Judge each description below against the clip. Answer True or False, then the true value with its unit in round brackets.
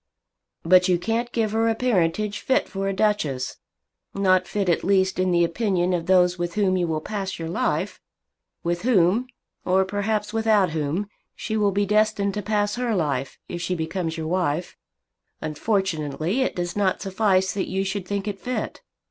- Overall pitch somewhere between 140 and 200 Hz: True (190 Hz)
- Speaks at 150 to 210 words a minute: True (180 wpm)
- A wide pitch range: False (3.2 semitones)